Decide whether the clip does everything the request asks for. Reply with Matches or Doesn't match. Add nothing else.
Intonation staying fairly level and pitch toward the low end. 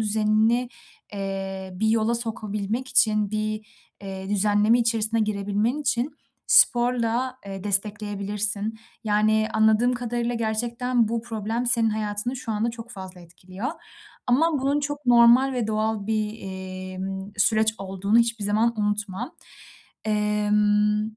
Doesn't match